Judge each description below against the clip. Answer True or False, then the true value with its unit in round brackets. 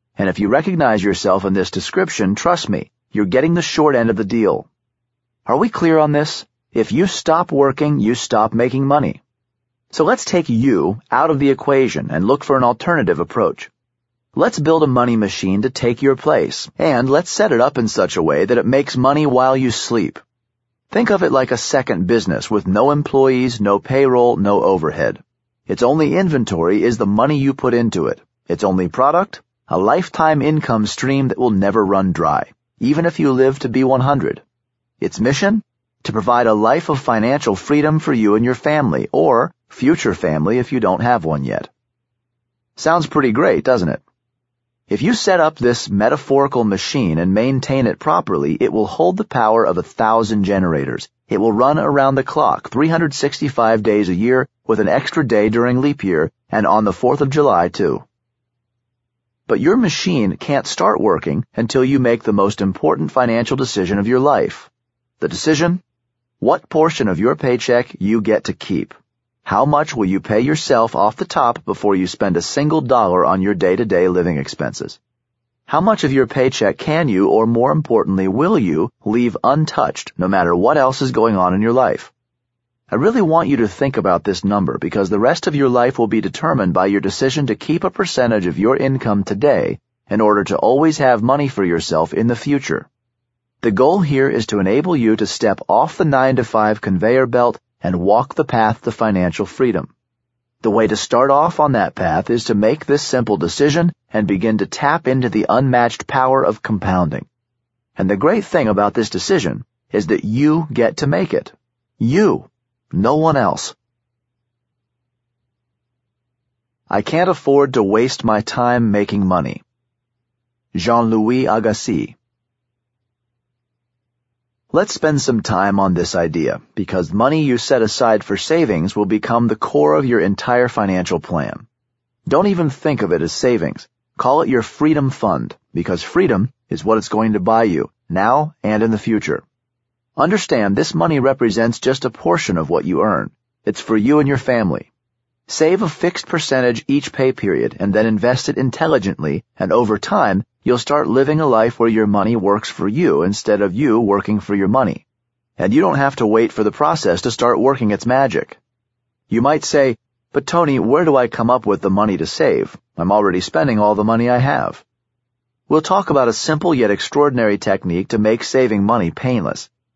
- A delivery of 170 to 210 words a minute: True (185 wpm)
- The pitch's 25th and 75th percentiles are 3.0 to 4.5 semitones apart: True (3.7 semitones)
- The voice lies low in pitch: True (120 Hz)